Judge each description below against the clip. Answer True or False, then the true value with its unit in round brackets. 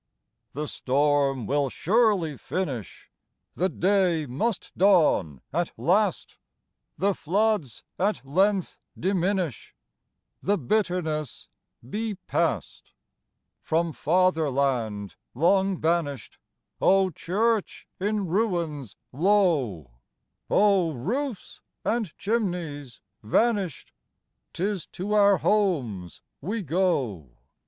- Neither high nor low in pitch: True (175 Hz)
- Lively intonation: True (6.1 semitones)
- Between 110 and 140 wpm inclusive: False (85 wpm)